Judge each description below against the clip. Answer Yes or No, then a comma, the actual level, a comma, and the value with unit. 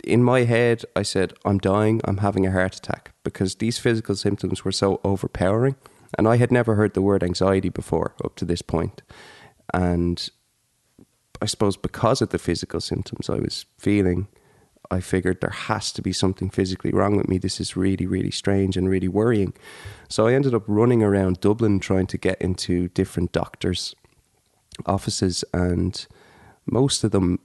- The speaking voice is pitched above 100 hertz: No, very low, 95 Hz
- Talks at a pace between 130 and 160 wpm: No, average, 175 wpm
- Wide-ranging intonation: No, average, 2.7 semitones